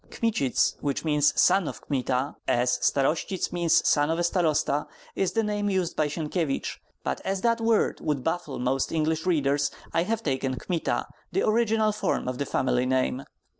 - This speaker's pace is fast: No, average, 170 wpm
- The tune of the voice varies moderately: No, wide, 5.7 semitones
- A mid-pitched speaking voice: Yes, medium, 160 Hz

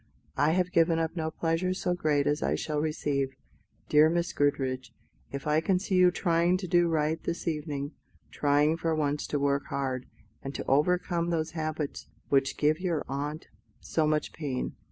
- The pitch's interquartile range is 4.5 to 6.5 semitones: No, average, 2.8 semitones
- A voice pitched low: No, medium, 155 Hz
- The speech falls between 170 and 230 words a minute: Yes, average, 175 wpm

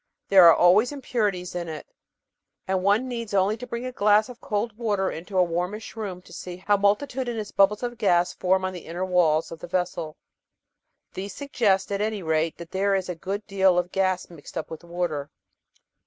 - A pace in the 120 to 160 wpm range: No, average, 200 wpm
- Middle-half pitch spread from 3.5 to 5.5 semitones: No, average, 3.1 semitones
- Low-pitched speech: No, high, 190 Hz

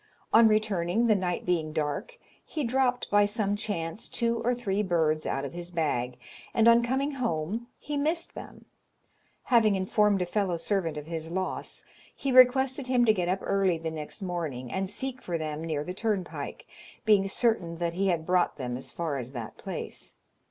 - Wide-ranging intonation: Yes, wide, 5.9 semitones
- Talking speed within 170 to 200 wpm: Yes, average, 185 wpm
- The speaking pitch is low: No, high, 190 Hz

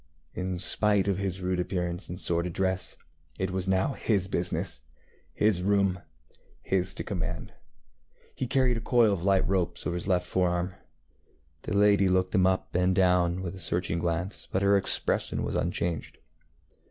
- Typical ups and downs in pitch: No, narrow, 1.8 semitones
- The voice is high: No, very low, 95 Hz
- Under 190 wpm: Yes, average, 165 wpm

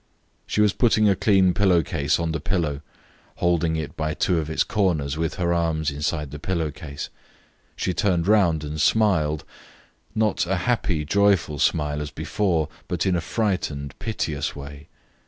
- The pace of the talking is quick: No, average, 165 wpm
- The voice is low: Yes, very low, 85 Hz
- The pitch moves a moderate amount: Yes, average, 4.2 semitones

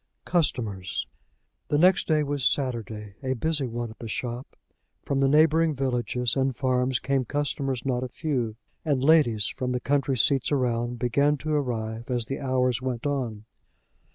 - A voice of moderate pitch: No, low, 130 Hz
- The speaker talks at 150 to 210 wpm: Yes, average, 160 wpm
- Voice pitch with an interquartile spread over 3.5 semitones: No, average, 3.1 semitones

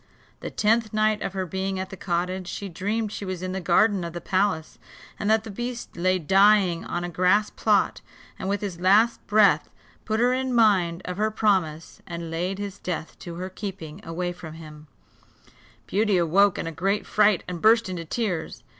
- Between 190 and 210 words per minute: Yes, average, 195 wpm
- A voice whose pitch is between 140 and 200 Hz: Yes, high, 190 Hz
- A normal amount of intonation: Yes, average, 3.4 semitones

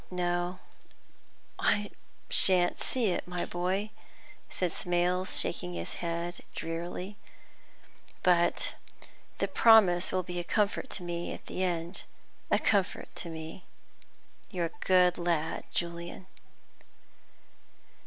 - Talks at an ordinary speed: No, slow, 115 wpm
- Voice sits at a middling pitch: Yes, medium, 175 Hz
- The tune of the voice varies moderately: No, narrow, 1.4 semitones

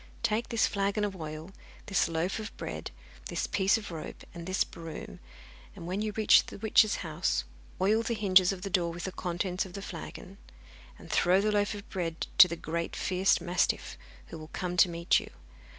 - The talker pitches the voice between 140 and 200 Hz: Yes, medium, 185 Hz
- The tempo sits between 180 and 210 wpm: Yes, average, 195 wpm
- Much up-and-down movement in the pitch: No, average, 3.2 semitones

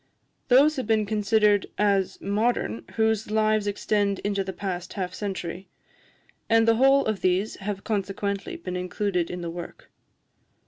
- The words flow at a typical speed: Yes, average, 145 wpm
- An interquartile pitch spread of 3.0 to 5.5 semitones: No, narrow, 2.5 semitones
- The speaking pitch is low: No, high, 205 Hz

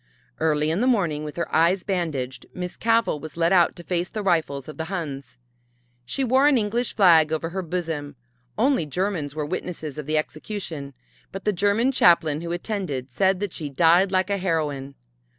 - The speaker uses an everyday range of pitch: Yes, average, 4.2 semitones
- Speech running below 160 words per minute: No, average, 185 wpm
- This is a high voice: No, medium, 170 Hz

